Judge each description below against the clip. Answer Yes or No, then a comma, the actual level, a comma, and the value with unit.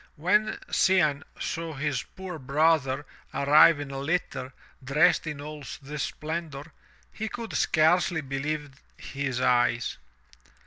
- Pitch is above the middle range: No, medium, 150 Hz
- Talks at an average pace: No, slow, 120 wpm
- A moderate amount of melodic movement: Yes, average, 3.1 semitones